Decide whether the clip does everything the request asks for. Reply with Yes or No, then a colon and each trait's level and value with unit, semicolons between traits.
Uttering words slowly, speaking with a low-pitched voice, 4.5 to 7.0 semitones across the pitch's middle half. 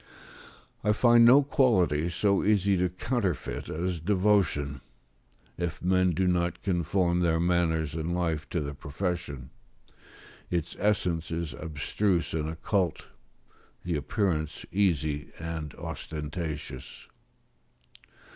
No: slow, 110 wpm; very low, 85 Hz; average, 3.3 semitones